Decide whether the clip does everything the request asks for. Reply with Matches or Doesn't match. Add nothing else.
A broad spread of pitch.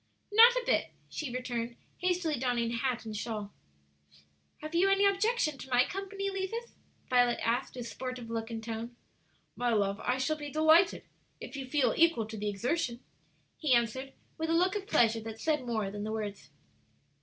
Matches